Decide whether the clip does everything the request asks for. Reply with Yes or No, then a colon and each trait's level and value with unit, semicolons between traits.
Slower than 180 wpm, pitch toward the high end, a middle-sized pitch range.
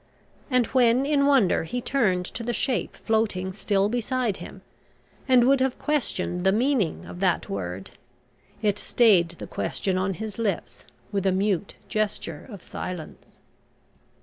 Yes: average, 150 wpm; high, 210 Hz; average, 5.0 semitones